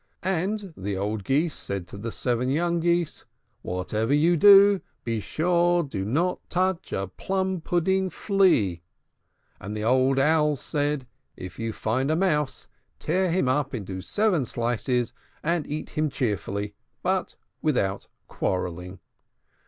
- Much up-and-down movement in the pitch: Yes, wide, 8.3 semitones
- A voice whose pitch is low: No, medium, 145 Hz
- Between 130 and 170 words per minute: Yes, average, 140 wpm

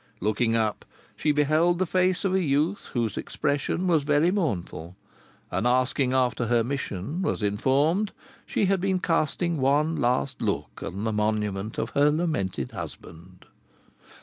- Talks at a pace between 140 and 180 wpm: Yes, average, 150 wpm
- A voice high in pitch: No, medium, 140 Hz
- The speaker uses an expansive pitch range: Yes, wide, 7.3 semitones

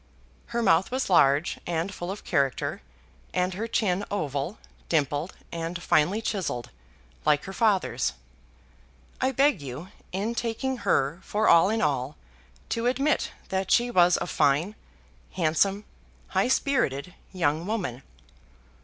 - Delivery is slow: Yes, slow, 130 wpm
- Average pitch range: No, wide, 6.3 semitones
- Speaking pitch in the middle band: Yes, medium, 180 Hz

